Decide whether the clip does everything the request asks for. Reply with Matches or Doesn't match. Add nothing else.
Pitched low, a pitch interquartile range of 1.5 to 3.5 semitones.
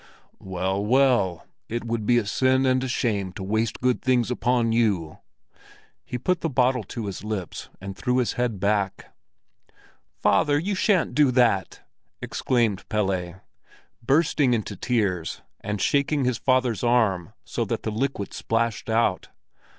Doesn't match